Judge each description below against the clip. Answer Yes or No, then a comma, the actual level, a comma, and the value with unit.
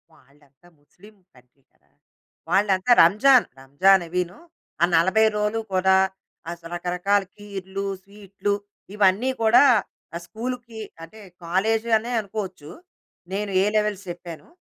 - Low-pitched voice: No, high, 195 Hz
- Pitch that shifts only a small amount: No, average, 3.4 semitones